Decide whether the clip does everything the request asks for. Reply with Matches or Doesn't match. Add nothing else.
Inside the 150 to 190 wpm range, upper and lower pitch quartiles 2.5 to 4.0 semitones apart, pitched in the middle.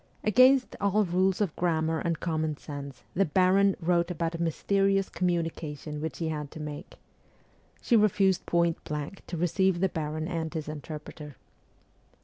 Matches